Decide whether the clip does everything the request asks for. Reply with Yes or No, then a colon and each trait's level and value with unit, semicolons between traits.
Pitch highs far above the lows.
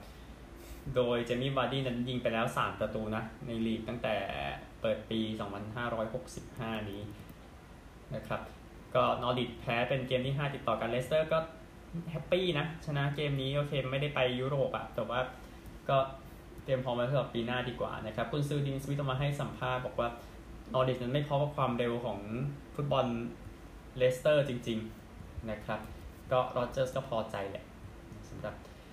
No: average, 3.8 semitones